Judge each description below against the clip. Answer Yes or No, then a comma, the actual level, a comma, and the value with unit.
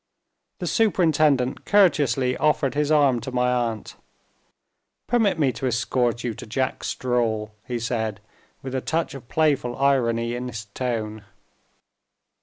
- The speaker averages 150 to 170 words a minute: No, slow, 135 wpm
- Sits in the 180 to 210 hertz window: No, low, 125 Hz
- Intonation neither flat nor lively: Yes, average, 3.5 semitones